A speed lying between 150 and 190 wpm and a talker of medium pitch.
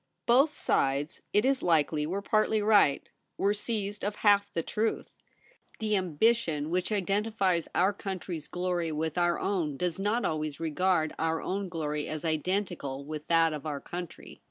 Yes: average, 155 wpm; medium, 180 Hz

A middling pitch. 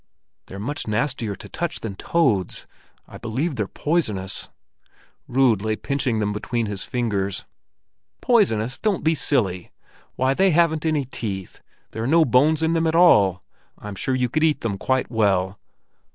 No: low, 125 Hz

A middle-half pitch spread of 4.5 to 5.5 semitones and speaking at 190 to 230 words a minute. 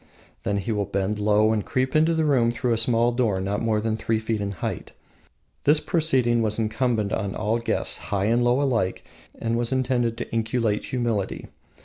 No: narrow, 2.6 semitones; average, 195 wpm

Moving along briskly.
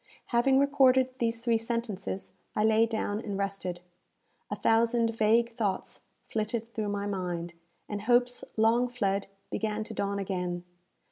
No: average, 140 wpm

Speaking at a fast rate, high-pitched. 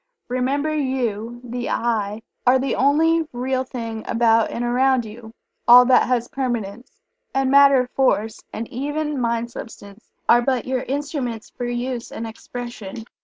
No: average, 145 wpm; high, 245 Hz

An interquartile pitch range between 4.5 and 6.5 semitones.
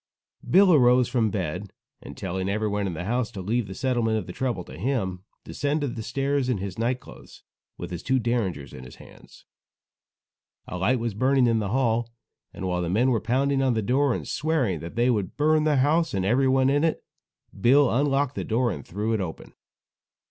Yes: average, 5.3 semitones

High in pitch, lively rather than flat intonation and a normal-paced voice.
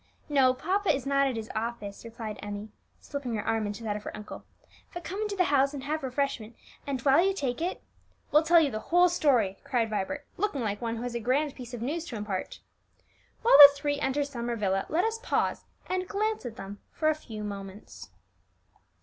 No: very high, 265 Hz; wide, 5.9 semitones; fast, 215 wpm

